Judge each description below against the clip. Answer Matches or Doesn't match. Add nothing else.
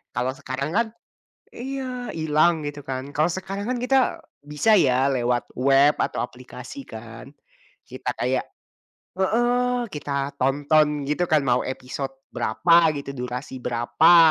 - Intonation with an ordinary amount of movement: Doesn't match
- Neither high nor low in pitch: Matches